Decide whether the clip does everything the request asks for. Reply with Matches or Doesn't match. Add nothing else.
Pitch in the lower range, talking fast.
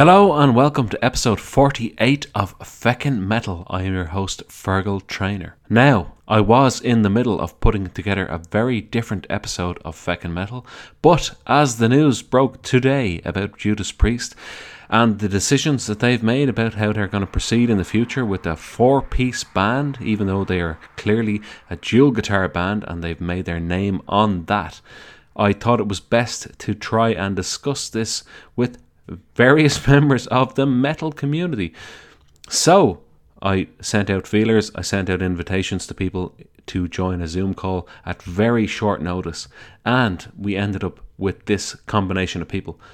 Doesn't match